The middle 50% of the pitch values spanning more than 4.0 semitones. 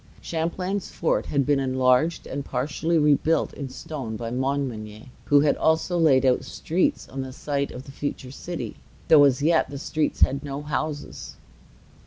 No: average, 3.2 semitones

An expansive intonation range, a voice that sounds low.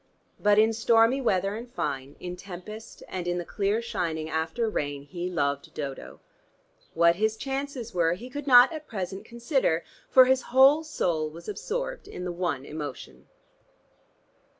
No: wide, 6.7 semitones; high, 195 Hz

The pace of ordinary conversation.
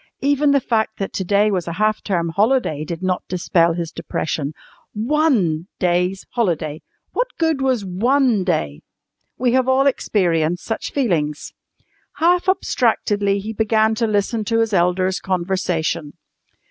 Yes: average, 145 wpm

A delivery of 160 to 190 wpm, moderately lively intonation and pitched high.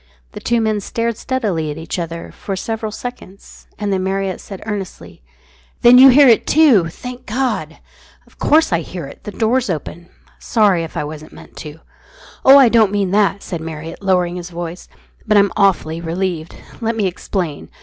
Yes: average, 180 wpm; average, 5.0 semitones; high, 195 Hz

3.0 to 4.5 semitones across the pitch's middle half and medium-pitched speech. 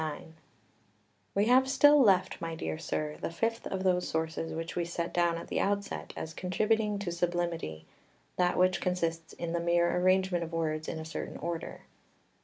No: narrow, 2.4 semitones; medium, 175 Hz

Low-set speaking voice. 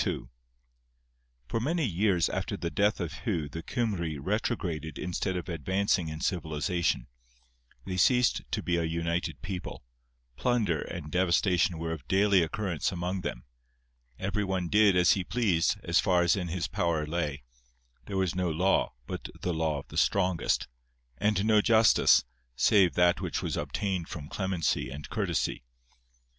Yes: very low, 90 Hz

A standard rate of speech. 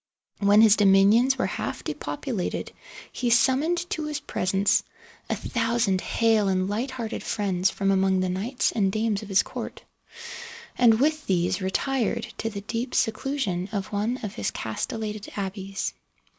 Yes: average, 150 wpm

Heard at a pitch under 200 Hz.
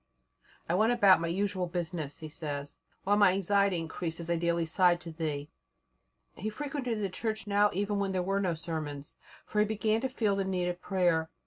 Yes: medium, 185 Hz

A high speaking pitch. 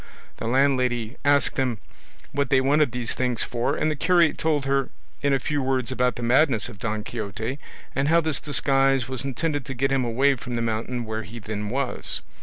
No: low, 130 Hz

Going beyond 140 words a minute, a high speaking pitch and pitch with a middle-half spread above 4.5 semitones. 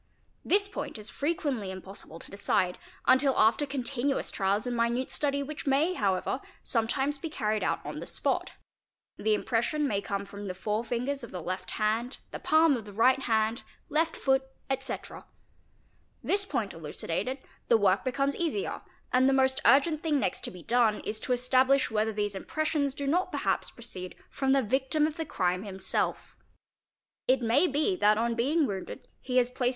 Yes: average, 180 wpm; very high, 250 Hz; average, 4.9 semitones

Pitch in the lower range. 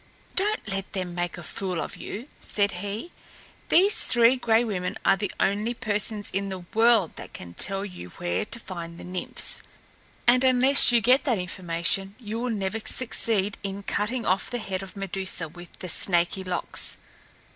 No: high, 200 Hz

